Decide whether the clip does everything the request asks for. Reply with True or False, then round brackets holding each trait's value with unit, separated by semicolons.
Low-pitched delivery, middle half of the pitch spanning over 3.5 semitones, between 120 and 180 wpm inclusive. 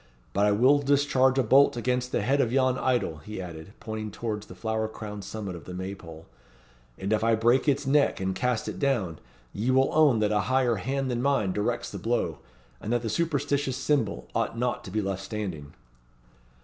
False (115 Hz; 4.5 semitones; 205 wpm)